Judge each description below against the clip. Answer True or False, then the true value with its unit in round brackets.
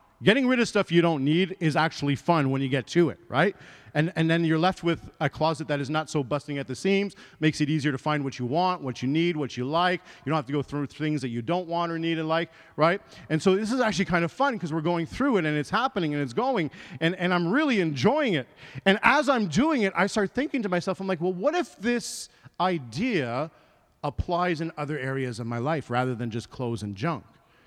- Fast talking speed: True (255 wpm)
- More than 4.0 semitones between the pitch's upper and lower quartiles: True (4.5 semitones)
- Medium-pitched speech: True (165 Hz)